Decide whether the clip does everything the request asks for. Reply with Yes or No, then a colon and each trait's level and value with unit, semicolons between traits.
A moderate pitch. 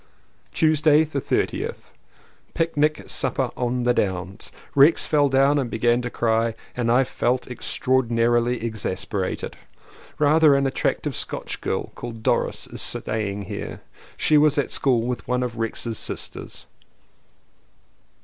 No: low, 125 Hz